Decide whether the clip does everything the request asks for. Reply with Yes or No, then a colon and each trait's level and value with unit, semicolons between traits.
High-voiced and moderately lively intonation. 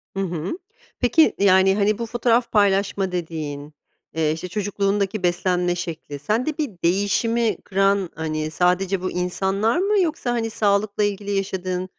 Yes: high, 195 Hz; average, 3.1 semitones